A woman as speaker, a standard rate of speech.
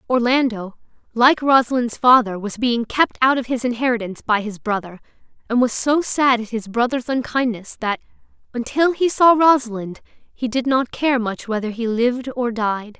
Yes: female; average, 170 wpm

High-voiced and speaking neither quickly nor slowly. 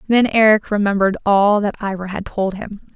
Yes: high, 205 Hz; average, 185 wpm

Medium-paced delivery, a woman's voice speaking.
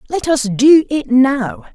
Yes: average, 170 wpm; female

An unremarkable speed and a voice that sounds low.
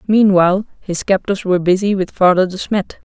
No: average, 175 wpm; high, 190 Hz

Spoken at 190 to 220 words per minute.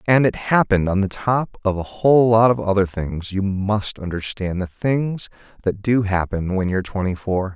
Yes: average, 200 wpm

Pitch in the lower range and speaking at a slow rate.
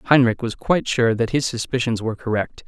No: low, 120 Hz; average, 200 wpm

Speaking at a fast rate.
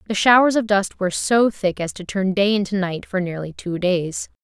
Yes: fast, 230 wpm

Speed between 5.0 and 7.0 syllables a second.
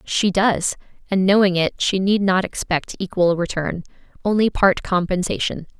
No: 4.6 syllables/s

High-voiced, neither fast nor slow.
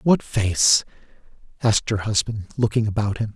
No: low, 110 Hz; average, 145 wpm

